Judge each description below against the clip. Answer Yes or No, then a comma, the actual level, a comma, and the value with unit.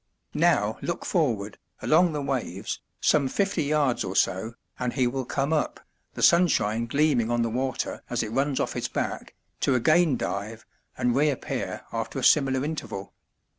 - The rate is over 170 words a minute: No, average, 165 wpm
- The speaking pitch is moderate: No, low, 130 Hz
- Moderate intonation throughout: Yes, average, 4.6 semitones